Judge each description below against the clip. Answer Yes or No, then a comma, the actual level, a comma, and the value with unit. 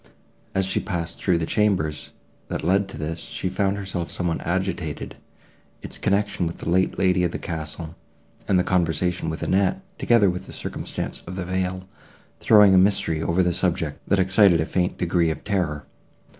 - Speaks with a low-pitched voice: Yes, very low, 90 Hz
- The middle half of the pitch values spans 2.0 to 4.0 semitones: Yes, narrow, 2.4 semitones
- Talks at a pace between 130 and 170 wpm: No, average, 180 wpm